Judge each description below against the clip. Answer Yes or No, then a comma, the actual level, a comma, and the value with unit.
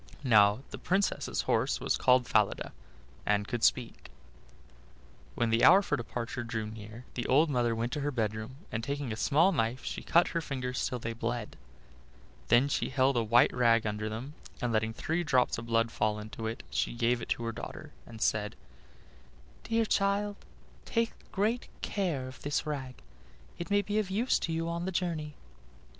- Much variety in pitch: Yes, wide, 6.2 semitones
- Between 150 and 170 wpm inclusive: No, average, 180 wpm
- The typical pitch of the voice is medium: No, low, 125 Hz